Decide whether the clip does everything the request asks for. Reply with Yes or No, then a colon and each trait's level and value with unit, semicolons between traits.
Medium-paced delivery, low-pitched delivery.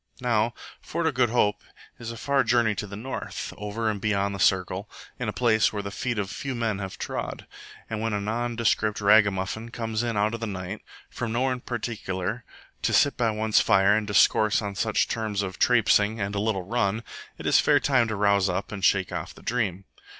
No: fast, 215 wpm; low, 110 Hz